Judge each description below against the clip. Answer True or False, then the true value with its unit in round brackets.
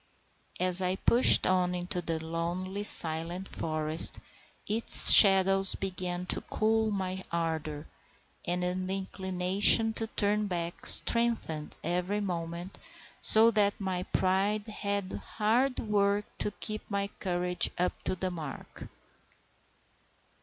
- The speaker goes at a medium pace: False (115 wpm)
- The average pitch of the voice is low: False (185 Hz)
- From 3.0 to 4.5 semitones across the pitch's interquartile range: False (2.6 semitones)